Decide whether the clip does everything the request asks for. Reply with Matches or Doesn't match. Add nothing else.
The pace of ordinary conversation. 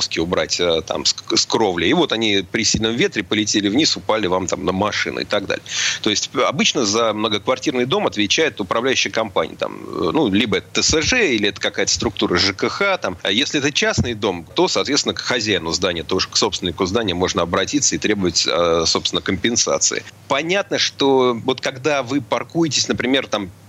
Doesn't match